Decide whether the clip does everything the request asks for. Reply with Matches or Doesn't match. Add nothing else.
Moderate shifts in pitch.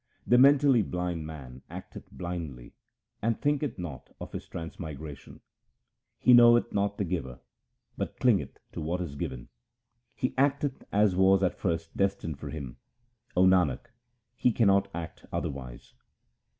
Doesn't match